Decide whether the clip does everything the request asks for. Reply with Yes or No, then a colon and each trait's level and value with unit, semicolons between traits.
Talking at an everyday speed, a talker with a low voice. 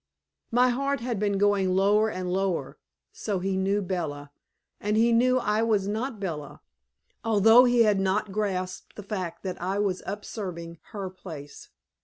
No: average, 165 wpm; high, 200 Hz